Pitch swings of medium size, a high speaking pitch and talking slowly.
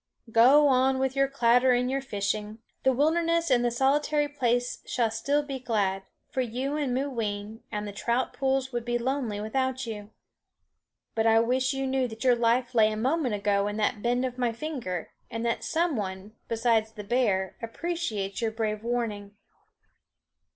No: average, 3.5 semitones; high, 240 Hz; average, 175 wpm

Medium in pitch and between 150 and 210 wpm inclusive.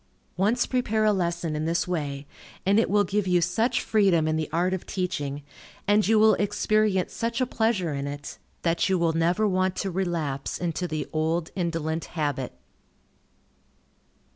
Yes: medium, 180 Hz; average, 165 wpm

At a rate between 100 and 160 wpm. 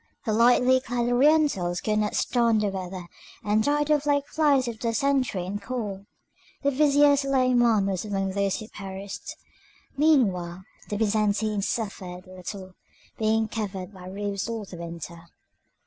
Yes: average, 145 wpm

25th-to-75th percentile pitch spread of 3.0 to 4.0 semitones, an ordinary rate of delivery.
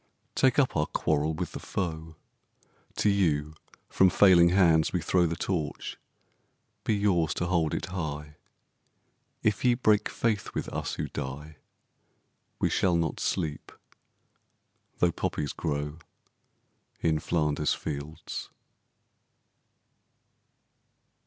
No: average, 3.7 semitones; slow, 115 wpm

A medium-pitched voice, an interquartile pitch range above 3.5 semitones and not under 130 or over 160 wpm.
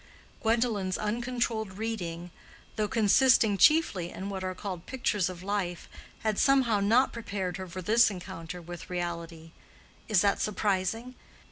No: high, 200 Hz; average, 3.9 semitones; slow, 135 wpm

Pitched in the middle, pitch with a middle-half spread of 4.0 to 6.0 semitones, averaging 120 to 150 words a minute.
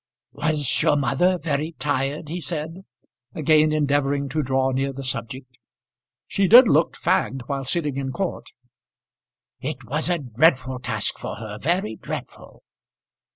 No: medium, 145 Hz; average, 3.1 semitones; average, 140 wpm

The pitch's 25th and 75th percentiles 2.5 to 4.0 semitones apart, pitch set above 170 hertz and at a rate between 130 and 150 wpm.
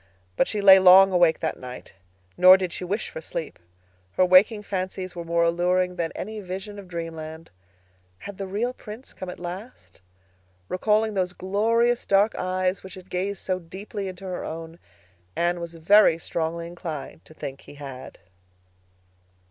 No: average, 2.8 semitones; medium, 185 Hz; average, 165 wpm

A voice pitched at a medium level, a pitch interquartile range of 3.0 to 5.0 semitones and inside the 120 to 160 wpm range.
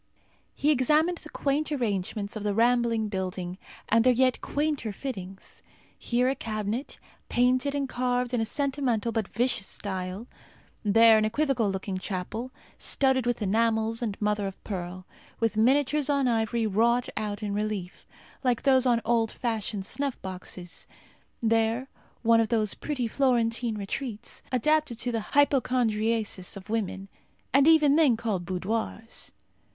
No: high, 230 Hz; average, 3.5 semitones; average, 145 wpm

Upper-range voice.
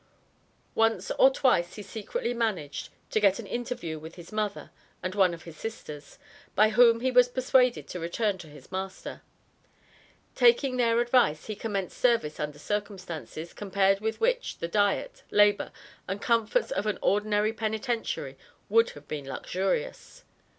Yes: high, 210 Hz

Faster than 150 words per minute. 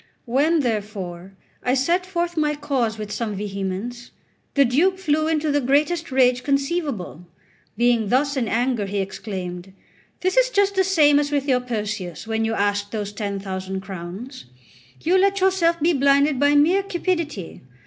Yes: average, 160 wpm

